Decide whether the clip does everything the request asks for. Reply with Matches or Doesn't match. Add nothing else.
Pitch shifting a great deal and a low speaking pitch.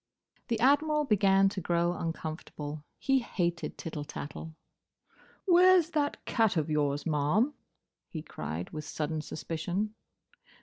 Doesn't match